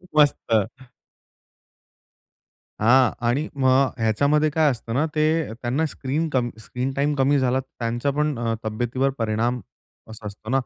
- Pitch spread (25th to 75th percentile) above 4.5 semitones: No, average, 3.7 semitones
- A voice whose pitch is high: No, low, 130 Hz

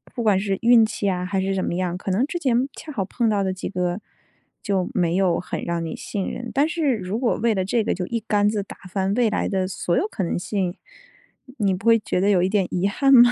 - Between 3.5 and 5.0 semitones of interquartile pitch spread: Yes, average, 3.8 semitones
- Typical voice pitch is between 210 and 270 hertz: No, high, 200 Hz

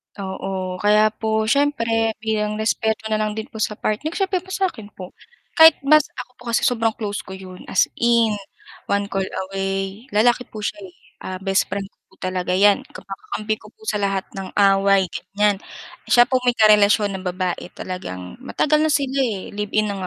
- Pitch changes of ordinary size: Yes, average, 3.0 semitones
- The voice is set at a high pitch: Yes, high, 210 Hz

